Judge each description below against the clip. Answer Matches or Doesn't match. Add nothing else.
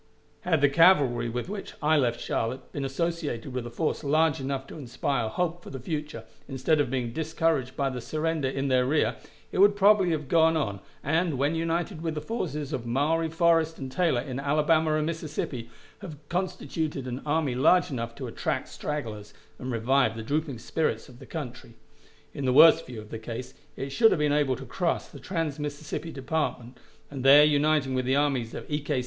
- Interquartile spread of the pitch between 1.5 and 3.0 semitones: Doesn't match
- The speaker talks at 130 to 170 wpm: Doesn't match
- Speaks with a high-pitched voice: Doesn't match